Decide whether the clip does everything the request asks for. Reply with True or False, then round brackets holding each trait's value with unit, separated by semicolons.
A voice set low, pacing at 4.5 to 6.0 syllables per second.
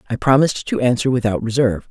False (120 Hz; 7.0 syllables/s)